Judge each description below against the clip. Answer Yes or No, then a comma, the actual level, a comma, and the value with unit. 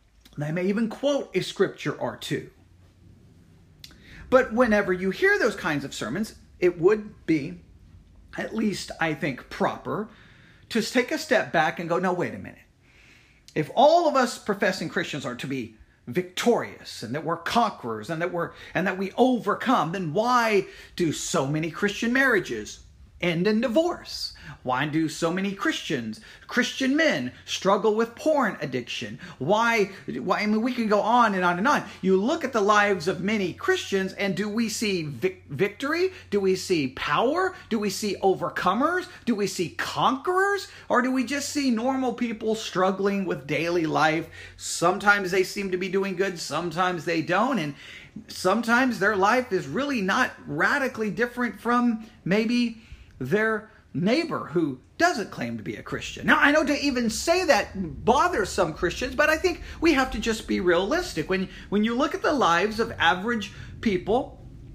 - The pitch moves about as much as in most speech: No, wide, 6.1 semitones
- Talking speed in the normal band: Yes, average, 170 wpm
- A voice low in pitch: No, high, 200 Hz